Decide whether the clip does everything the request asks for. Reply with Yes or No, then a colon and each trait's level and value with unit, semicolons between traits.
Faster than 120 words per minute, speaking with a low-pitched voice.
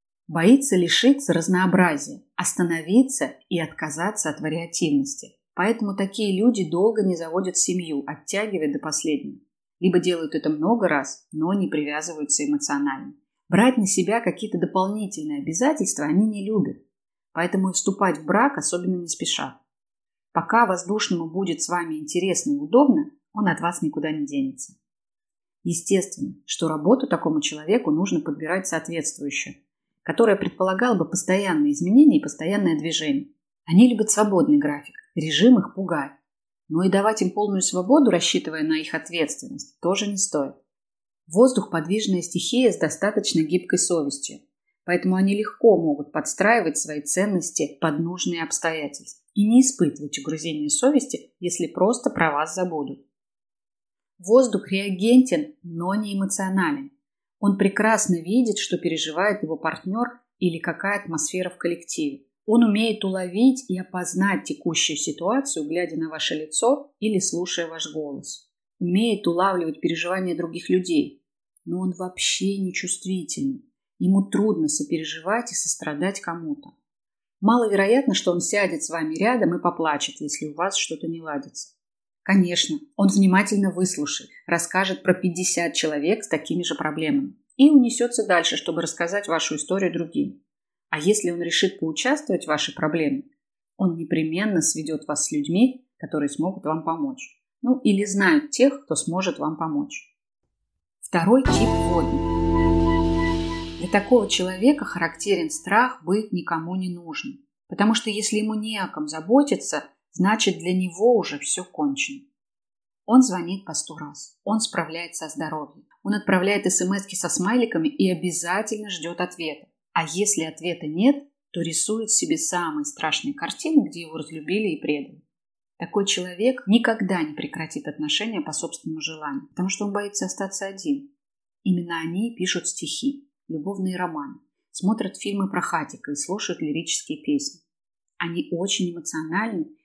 No: average, 140 wpm; medium, 185 Hz